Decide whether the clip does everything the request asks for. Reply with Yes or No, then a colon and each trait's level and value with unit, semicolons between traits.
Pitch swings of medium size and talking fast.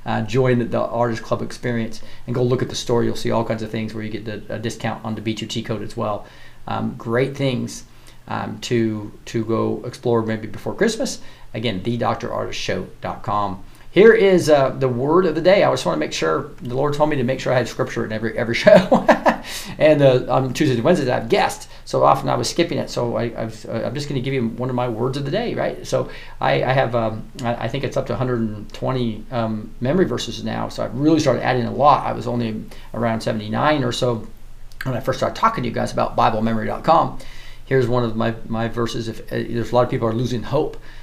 No: narrow, 2.2 semitones; fast, 235 wpm